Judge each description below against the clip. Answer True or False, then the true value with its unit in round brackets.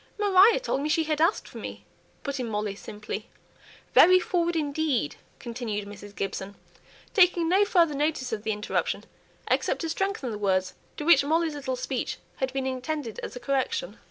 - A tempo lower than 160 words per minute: False (175 wpm)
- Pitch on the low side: False (280 Hz)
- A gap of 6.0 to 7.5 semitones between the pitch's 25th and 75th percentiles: True (7.1 semitones)